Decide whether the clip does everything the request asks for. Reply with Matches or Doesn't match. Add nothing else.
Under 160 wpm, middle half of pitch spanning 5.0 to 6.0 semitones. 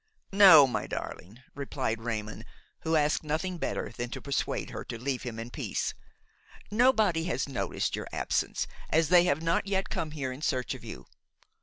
Doesn't match